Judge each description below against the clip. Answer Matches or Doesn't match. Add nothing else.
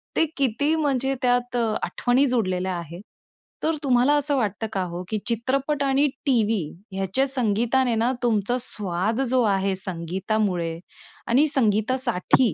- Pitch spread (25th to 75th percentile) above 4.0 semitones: Matches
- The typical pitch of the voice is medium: Doesn't match